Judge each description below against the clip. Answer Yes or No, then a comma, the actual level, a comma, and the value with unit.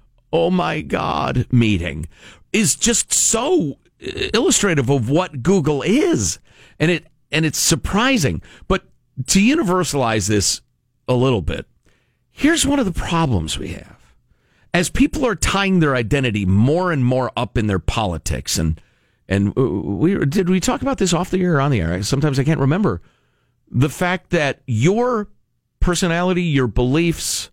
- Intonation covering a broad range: Yes, wide, 7.7 semitones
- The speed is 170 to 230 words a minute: No, average, 155 wpm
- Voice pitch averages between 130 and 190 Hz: Yes, medium, 140 Hz